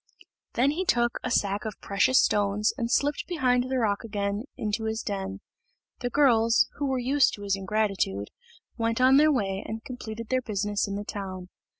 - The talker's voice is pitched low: No, high, 220 Hz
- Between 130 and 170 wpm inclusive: No, average, 185 wpm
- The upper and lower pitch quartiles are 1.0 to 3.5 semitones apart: No, average, 3.9 semitones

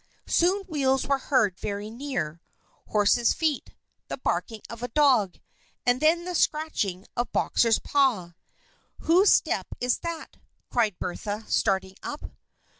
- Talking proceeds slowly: Yes, slow, 130 wpm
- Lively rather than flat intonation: Yes, wide, 6.6 semitones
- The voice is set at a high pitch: Yes, high, 245 Hz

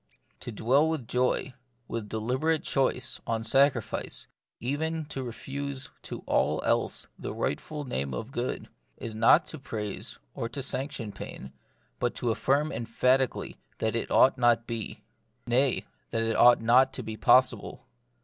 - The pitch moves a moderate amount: Yes, average, 3.3 semitones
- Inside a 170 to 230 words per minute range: No, average, 160 wpm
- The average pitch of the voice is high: No, low, 125 Hz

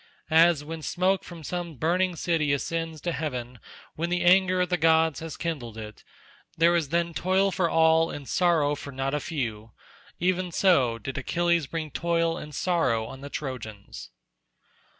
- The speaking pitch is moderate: Yes, medium, 160 Hz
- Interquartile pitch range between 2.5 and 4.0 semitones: Yes, average, 3.7 semitones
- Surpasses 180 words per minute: No, average, 165 wpm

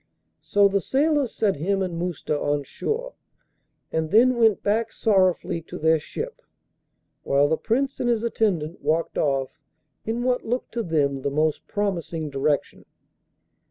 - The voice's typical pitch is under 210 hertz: Yes, high, 190 Hz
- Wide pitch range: Yes, wide, 6.9 semitones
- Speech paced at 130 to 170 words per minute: Yes, average, 150 wpm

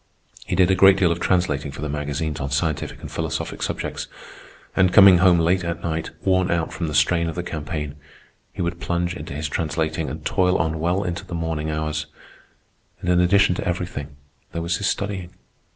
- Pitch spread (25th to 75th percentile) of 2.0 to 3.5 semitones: Yes, average, 2.7 semitones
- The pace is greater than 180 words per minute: Yes, average, 200 wpm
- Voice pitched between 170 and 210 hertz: No, very low, 85 Hz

